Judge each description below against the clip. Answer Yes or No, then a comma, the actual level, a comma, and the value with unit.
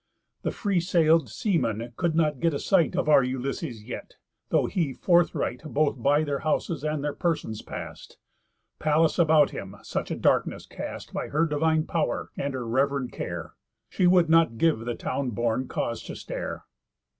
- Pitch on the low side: No, medium, 150 Hz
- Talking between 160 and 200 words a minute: Yes, average, 170 wpm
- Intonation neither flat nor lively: Yes, average, 4.5 semitones